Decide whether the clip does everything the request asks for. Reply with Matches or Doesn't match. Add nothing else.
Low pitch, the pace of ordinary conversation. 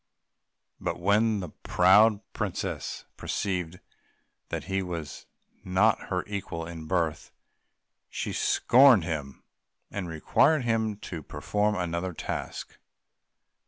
Doesn't match